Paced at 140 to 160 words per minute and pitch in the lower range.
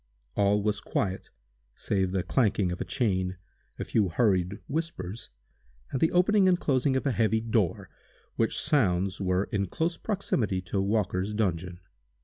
Yes: average, 150 wpm; low, 105 Hz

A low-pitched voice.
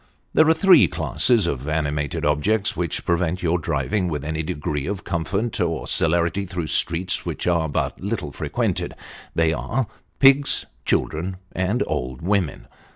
Yes: very low, 85 Hz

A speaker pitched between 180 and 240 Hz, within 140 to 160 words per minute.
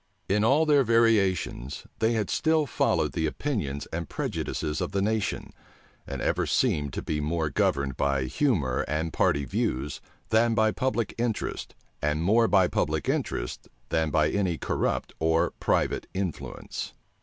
No: very low, 90 Hz; average, 150 wpm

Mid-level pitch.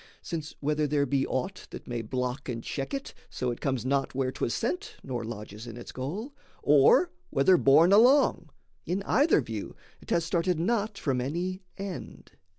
Yes: medium, 150 Hz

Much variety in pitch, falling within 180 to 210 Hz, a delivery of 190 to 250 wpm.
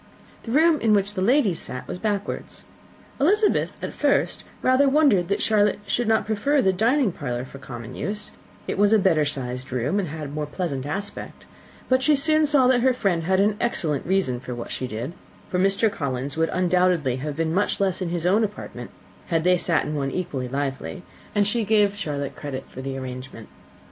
Yes: wide, 7.2 semitones; medium, 185 Hz; average, 200 wpm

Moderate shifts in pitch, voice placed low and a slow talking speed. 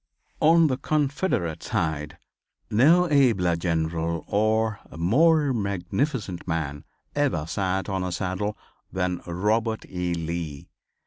No: wide, 6.9 semitones; very low, 95 Hz; slow, 110 wpm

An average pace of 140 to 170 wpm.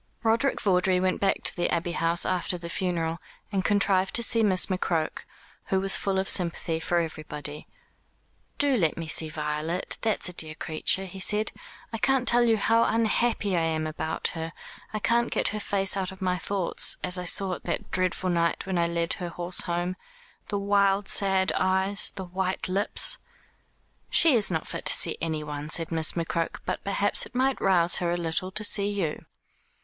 No: average, 190 wpm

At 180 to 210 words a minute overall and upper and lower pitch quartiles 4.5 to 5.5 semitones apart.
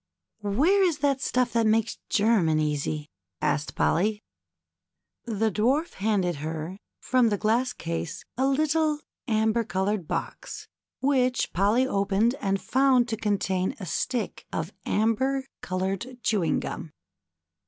No: slow, 135 wpm; average, 5.1 semitones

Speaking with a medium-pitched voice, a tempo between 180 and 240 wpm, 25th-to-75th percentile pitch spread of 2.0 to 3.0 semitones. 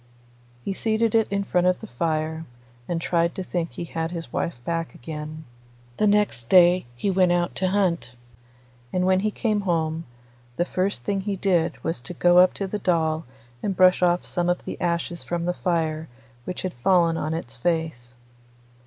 Yes: medium, 175 Hz; average, 190 wpm; narrow, 2.4 semitones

